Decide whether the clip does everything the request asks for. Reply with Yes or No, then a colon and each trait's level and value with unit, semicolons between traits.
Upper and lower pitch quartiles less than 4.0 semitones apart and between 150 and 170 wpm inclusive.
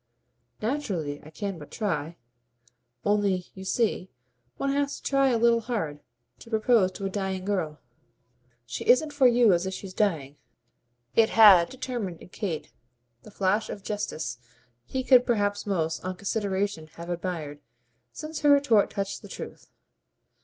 No: average, 4.9 semitones; average, 155 wpm